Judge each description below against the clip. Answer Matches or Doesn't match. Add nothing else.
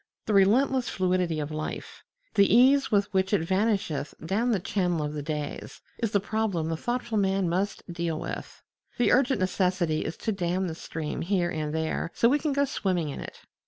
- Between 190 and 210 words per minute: Matches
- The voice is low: Doesn't match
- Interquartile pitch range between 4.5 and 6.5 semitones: Matches